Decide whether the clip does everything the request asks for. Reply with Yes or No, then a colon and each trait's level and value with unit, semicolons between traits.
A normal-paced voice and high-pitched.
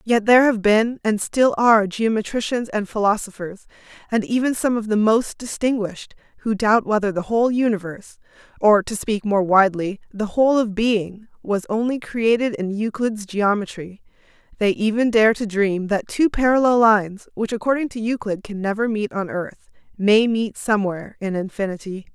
Yes: average, 165 wpm; high, 215 Hz